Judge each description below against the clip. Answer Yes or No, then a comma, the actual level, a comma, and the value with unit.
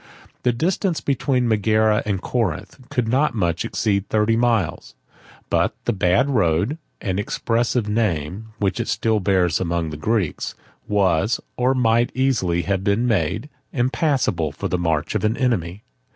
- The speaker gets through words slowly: No, average, 150 wpm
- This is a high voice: No, low, 105 Hz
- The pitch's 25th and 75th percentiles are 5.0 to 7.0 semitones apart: Yes, average, 5.3 semitones